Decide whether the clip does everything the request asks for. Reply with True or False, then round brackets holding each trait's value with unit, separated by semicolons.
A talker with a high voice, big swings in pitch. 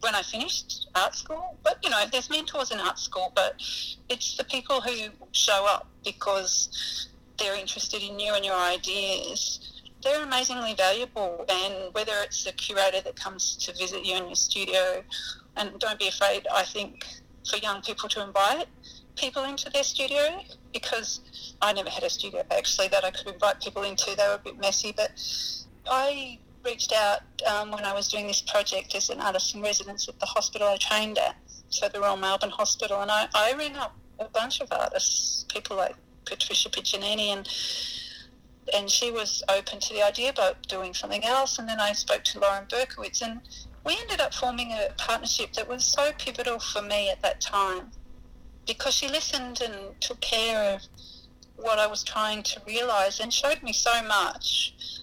False (210 Hz; 4.3 semitones)